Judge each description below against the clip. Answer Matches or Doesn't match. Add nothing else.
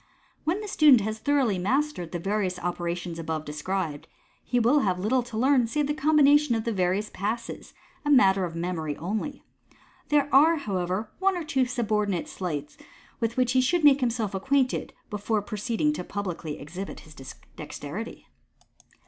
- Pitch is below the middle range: Doesn't match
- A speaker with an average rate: Matches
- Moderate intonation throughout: Doesn't match